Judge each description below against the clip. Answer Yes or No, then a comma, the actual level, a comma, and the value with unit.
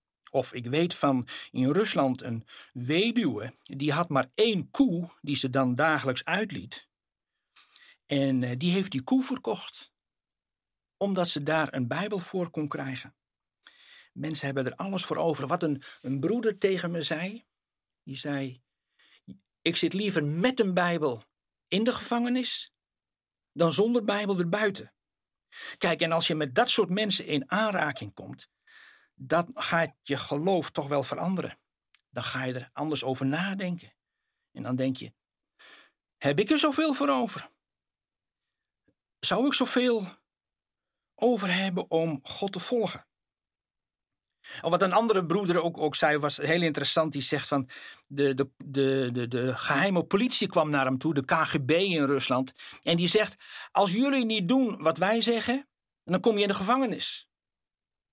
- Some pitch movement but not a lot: No, wide, 6.5 semitones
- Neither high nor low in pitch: Yes, medium, 165 Hz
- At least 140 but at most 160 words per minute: Yes, average, 155 wpm